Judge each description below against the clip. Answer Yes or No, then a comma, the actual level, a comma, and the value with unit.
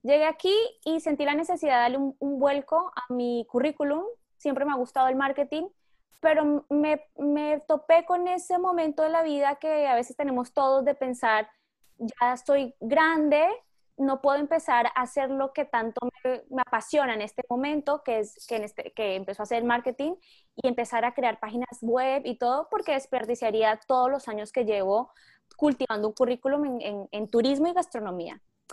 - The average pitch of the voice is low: No, very high, 270 Hz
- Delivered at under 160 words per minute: No, average, 185 wpm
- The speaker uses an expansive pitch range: No, average, 3.9 semitones